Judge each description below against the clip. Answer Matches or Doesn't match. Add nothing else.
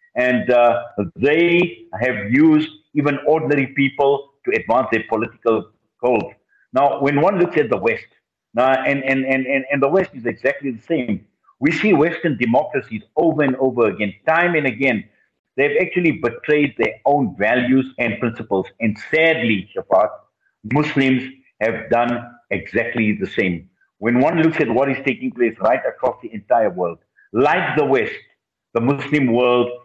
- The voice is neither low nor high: Doesn't match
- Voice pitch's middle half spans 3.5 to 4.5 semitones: Matches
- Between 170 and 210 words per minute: Doesn't match